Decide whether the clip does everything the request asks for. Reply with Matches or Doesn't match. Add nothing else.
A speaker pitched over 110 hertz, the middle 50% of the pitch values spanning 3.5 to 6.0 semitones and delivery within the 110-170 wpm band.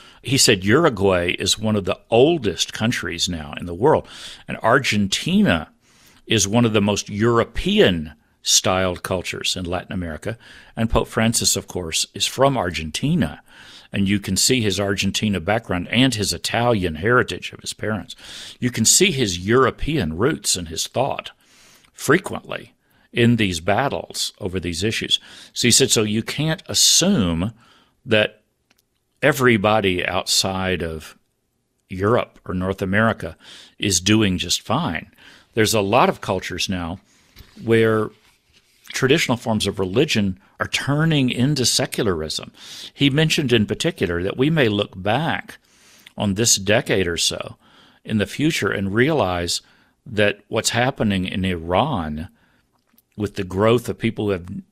Doesn't match